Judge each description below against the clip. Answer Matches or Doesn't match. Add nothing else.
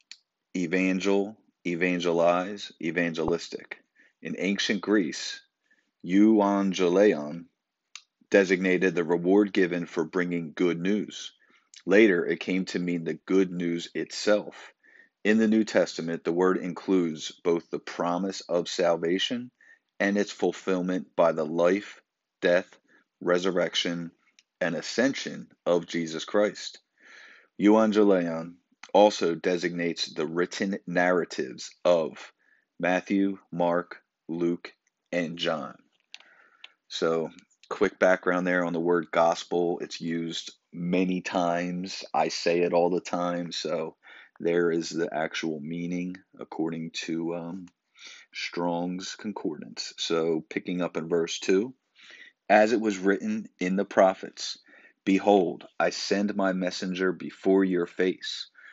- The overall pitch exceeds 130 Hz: Doesn't match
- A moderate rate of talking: Doesn't match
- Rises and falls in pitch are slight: Matches